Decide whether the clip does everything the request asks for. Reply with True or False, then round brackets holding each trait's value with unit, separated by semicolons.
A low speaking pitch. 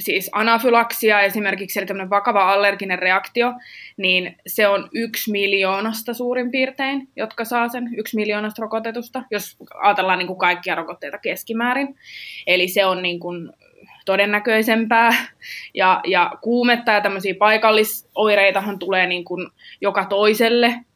False (210 Hz)